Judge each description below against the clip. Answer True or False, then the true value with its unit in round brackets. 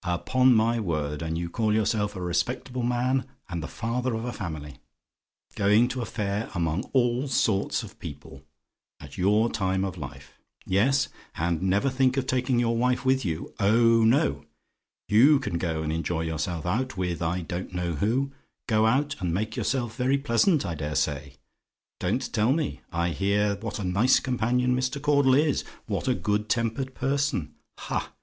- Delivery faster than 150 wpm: True (175 wpm)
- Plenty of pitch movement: True (6.3 semitones)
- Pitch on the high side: False (110 Hz)